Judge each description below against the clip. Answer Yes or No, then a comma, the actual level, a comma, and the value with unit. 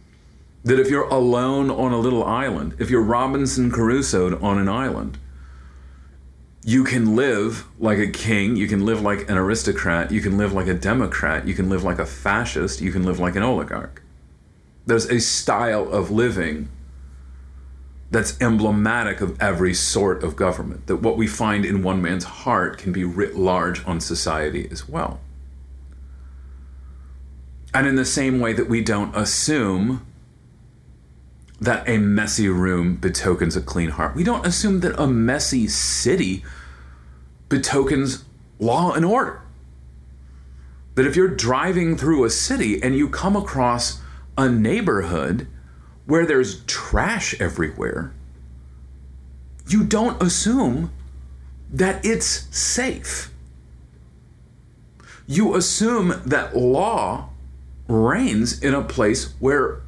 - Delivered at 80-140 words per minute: Yes, slow, 135 wpm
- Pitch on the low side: Yes, very low, 90 Hz